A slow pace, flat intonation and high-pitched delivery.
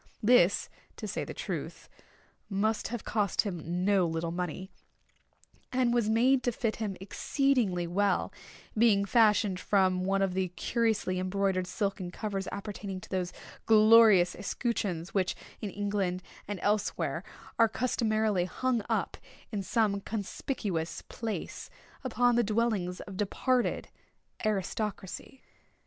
No: slow, 125 wpm; average, 3.3 semitones; high, 205 Hz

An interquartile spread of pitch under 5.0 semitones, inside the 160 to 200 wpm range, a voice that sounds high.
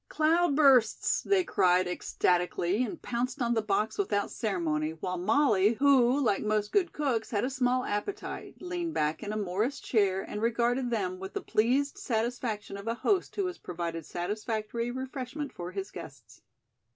No: average, 5.3 semitones; average, 165 wpm; high, 225 Hz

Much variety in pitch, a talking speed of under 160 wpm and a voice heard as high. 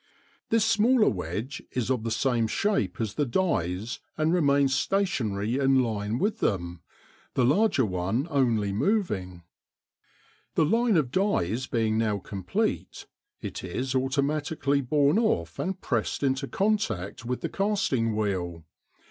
No: wide, 7.2 semitones; slow, 135 wpm; low, 130 Hz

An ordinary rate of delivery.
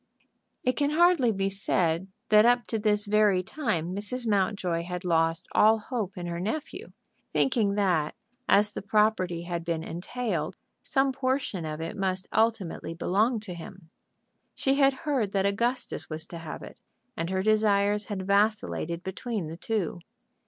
Yes: average, 160 wpm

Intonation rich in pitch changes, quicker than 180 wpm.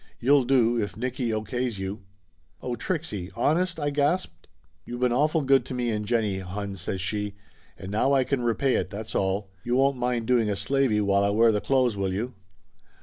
No: average, 4.6 semitones; fast, 205 wpm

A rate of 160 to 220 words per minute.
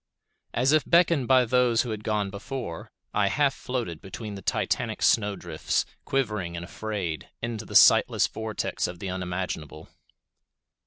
No: average, 145 wpm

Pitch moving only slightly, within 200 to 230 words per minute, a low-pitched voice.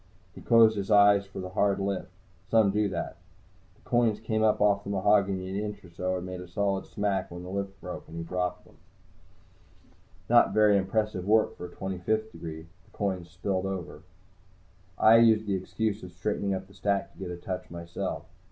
Yes: narrow, 2.3 semitones; fast, 205 wpm; low, 100 Hz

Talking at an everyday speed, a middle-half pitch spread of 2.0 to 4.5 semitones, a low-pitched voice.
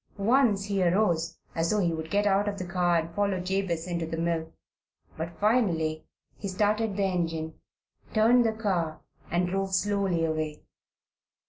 No: average, 160 wpm; average, 3.6 semitones; medium, 185 Hz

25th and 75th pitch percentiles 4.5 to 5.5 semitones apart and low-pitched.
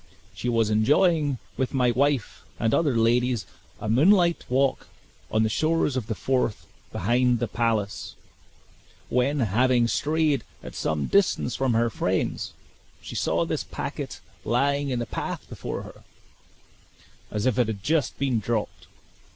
No: average, 3.8 semitones; low, 125 Hz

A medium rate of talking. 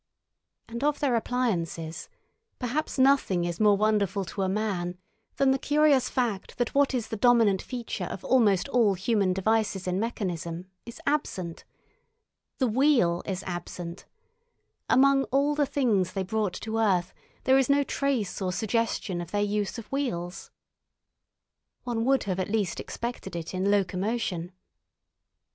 Yes: average, 145 wpm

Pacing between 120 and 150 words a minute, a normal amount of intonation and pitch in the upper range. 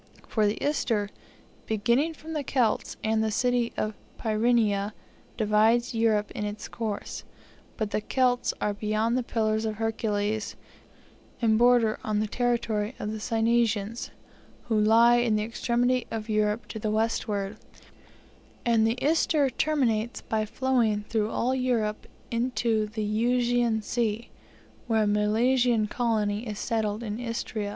No: average, 140 wpm; narrow, 2.1 semitones; high, 225 Hz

